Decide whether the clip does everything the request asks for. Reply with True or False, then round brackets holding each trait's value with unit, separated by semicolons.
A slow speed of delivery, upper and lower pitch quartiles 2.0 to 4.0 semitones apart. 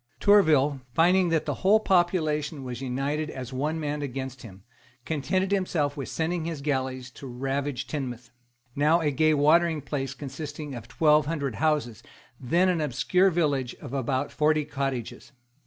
False (155 wpm; 3.4 semitones)